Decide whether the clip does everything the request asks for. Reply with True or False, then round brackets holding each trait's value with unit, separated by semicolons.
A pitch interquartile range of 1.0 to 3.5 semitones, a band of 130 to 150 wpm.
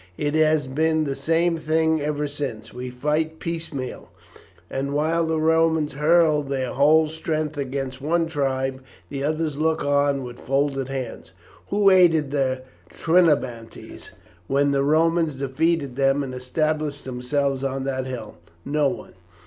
True (2.9 semitones; 140 wpm)